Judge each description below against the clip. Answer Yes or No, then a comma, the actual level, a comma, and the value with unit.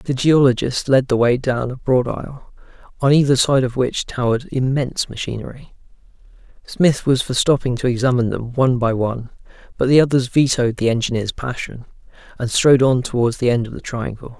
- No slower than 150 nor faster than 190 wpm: Yes, average, 180 wpm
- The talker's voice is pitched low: Yes, low, 125 Hz